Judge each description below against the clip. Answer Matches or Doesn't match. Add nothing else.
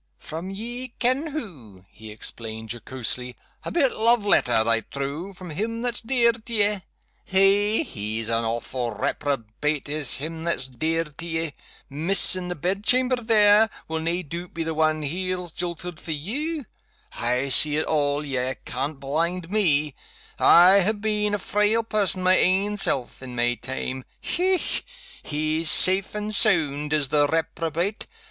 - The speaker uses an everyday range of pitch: Doesn't match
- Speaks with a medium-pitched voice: Matches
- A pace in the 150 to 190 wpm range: Matches